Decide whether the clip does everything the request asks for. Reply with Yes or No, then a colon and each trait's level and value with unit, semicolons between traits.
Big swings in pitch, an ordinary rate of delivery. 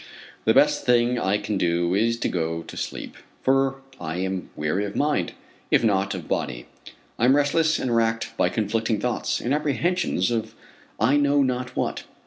Yes: wide, 5.9 semitones; average, 175 wpm